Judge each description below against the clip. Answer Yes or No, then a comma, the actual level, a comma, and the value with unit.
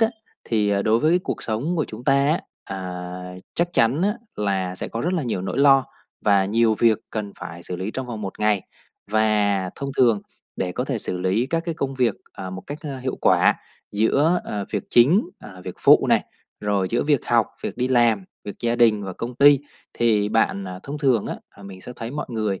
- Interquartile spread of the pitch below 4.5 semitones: No, average, 5.1 semitones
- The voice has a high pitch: No, low, 115 Hz